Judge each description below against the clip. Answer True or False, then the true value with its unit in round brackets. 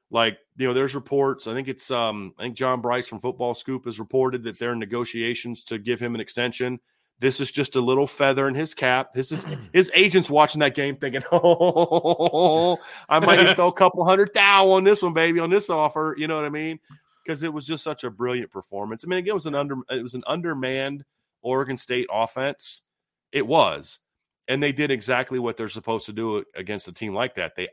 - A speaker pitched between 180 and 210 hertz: False (135 Hz)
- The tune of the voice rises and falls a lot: False (4.6 semitones)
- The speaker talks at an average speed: False (225 wpm)